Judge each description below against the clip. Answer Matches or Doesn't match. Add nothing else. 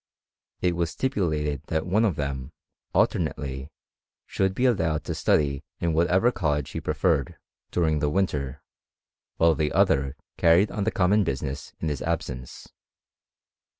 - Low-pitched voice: Matches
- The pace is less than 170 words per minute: Matches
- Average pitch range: Matches